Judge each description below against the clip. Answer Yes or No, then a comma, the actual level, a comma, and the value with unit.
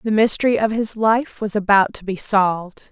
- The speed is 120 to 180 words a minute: No, fast, 205 wpm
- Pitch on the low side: No, high, 210 Hz